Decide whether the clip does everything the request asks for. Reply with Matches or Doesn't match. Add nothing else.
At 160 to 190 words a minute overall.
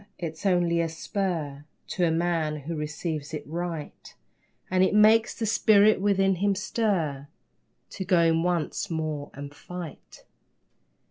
Doesn't match